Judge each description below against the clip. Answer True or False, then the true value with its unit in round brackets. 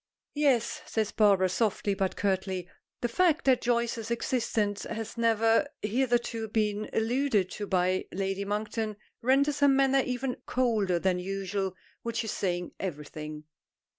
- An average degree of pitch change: True (3.9 semitones)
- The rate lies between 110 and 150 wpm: True (135 wpm)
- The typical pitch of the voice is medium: False (220 Hz)